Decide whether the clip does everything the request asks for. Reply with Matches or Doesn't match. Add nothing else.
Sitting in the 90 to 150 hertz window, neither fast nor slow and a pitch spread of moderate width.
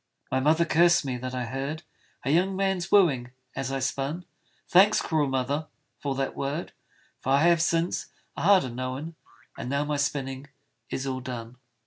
Matches